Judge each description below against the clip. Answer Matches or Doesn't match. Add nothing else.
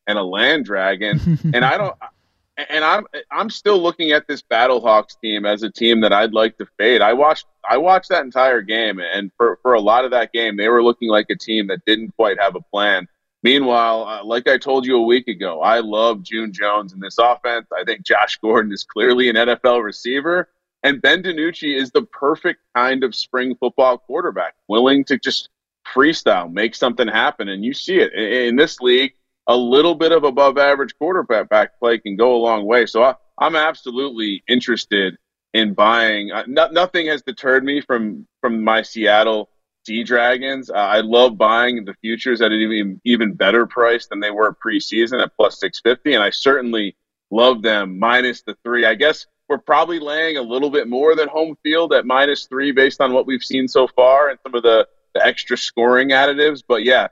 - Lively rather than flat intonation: Doesn't match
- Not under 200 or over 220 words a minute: Matches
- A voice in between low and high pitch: Doesn't match